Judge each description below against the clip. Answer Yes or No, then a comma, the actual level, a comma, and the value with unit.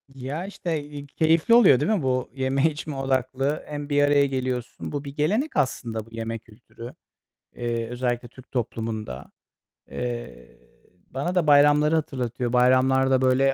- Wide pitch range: No, average, 3.2 semitones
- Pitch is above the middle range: No, low, 135 Hz